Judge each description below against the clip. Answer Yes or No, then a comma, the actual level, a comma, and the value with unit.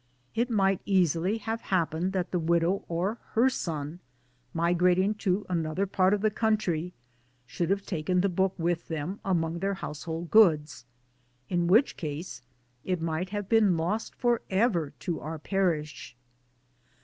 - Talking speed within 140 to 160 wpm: Yes, average, 150 wpm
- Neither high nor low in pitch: Yes, medium, 180 Hz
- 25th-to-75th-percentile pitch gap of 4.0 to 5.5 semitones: No, average, 3.3 semitones